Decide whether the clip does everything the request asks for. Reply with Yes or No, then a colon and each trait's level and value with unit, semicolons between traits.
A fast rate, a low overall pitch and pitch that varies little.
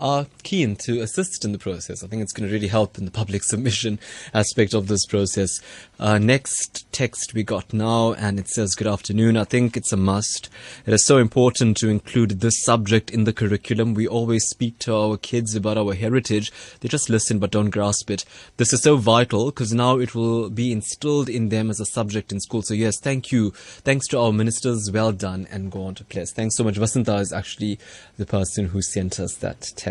Yes: fast, 220 wpm; low, 110 Hz; narrow, 2.3 semitones